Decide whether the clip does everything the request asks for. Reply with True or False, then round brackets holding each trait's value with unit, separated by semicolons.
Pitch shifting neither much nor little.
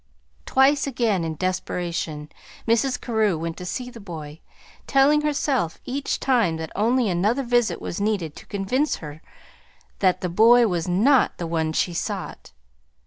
False (6.7 semitones)